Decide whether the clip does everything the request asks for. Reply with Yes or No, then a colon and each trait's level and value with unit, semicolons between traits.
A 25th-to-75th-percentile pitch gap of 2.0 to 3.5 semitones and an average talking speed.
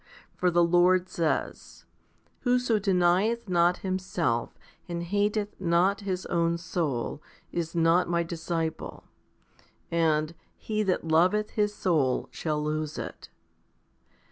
No: average, 2.7 semitones; slow, 115 wpm